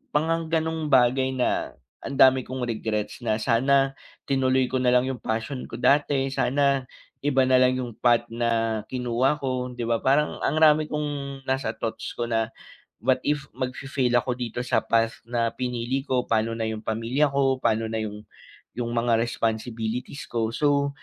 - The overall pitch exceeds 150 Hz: No, low, 125 Hz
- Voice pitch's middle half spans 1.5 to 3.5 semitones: Yes, average, 2.8 semitones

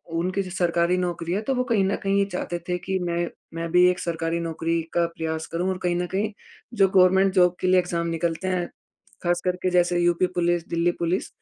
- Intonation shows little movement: Yes, narrow, 1.6 semitones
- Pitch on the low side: No, medium, 175 Hz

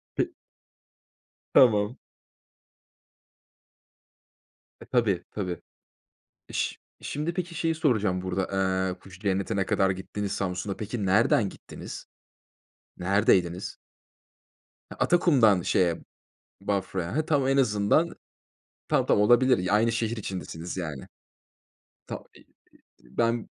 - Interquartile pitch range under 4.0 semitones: No, average, 4.5 semitones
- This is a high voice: No, low, 105 Hz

